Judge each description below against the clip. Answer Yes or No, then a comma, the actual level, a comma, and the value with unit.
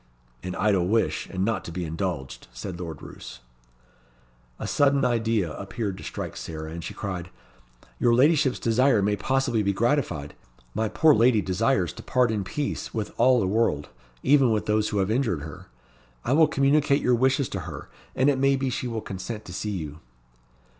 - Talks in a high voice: No, low, 110 Hz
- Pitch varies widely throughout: Yes, wide, 5.8 semitones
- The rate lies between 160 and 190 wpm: Yes, average, 185 wpm